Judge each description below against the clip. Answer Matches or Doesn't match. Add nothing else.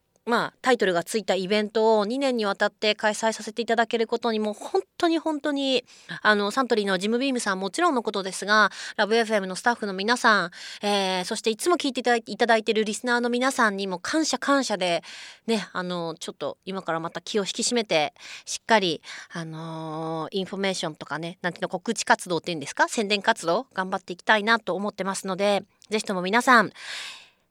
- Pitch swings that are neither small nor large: Matches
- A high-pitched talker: Matches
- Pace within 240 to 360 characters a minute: Doesn't match